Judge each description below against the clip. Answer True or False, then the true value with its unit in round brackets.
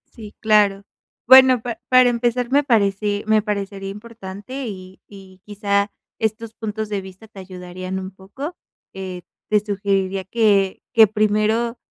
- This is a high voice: True (210 Hz)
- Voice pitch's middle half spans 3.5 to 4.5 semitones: False (2.7 semitones)